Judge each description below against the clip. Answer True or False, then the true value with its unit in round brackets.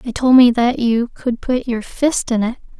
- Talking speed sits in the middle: False (235 wpm)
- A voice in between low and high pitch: False (240 Hz)